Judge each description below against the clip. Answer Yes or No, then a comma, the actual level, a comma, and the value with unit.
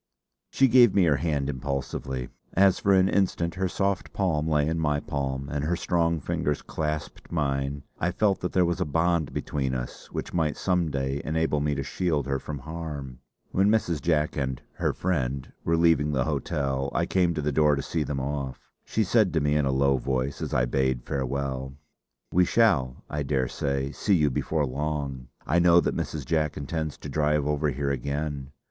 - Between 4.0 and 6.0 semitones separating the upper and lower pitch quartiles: No, average, 3.6 semitones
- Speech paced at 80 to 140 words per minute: No, average, 195 wpm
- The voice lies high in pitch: No, very low, 75 Hz